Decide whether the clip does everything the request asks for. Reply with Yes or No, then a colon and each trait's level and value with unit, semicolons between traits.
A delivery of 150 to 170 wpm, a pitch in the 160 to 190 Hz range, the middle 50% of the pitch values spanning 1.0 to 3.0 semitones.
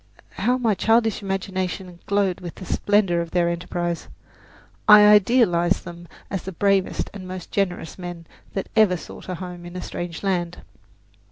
Yes: average, 160 wpm; medium, 185 Hz; narrow, 2.6 semitones